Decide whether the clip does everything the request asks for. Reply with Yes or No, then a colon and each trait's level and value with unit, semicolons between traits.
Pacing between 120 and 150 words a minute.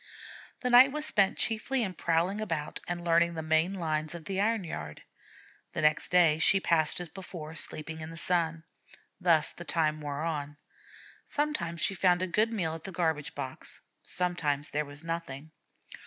No: average, 175 wpm